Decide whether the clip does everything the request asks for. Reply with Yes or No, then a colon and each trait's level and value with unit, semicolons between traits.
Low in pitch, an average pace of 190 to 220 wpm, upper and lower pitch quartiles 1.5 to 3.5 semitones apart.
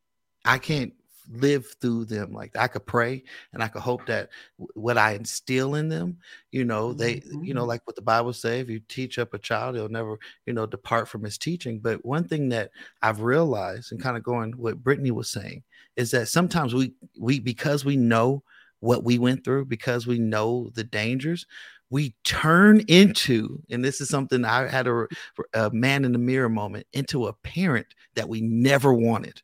Yes: low, 120 Hz; average, 200 wpm; average, 2.9 semitones